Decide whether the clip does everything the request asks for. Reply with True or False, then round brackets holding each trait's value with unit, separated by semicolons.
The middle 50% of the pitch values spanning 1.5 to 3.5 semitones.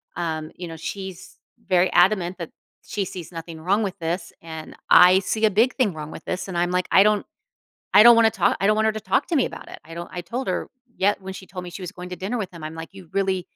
True (2.9 semitones)